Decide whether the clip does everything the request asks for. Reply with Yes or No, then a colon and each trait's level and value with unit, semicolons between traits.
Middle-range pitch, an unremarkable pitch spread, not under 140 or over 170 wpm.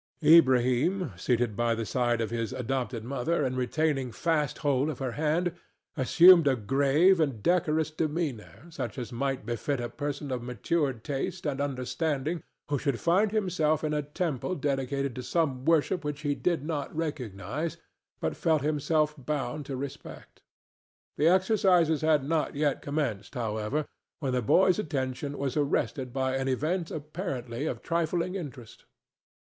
Yes: medium, 145 Hz; average, 3.9 semitones; average, 155 wpm